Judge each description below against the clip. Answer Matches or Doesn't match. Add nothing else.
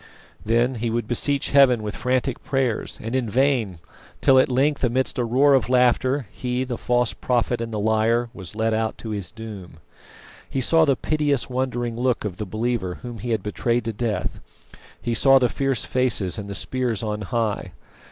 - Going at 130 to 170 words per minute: Doesn't match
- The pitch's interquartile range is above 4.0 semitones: Doesn't match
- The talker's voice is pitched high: Doesn't match